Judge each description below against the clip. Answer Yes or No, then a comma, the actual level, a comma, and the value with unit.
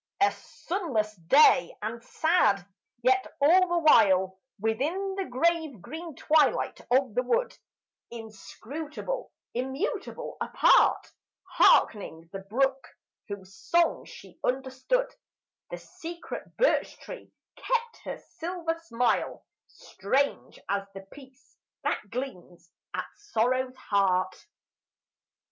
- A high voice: Yes, very high, 265 Hz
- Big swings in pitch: Yes, wide, 7.9 semitones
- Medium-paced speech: No, slow, 105 wpm